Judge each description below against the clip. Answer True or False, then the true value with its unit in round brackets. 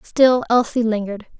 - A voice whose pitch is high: True (230 Hz)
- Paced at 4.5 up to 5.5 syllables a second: True (5.1 syllables/s)